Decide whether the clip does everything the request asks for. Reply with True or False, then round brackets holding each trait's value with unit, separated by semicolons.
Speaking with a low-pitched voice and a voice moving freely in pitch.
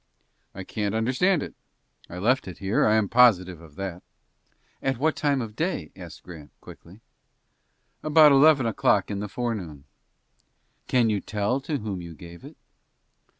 True (105 Hz; 6.1 semitones)